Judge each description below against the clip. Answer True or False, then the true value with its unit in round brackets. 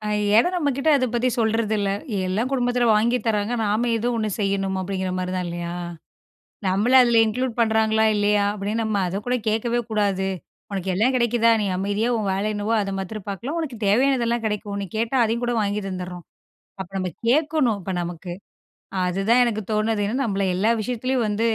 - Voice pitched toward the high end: True (215 Hz)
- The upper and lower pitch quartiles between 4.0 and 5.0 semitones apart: False (3.2 semitones)